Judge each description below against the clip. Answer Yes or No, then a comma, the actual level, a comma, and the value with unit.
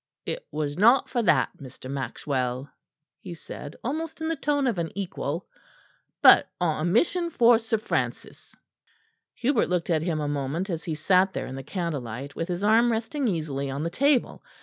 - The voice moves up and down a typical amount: No, wide, 8.2 semitones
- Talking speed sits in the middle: Yes, average, 180 wpm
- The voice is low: No, medium, 175 Hz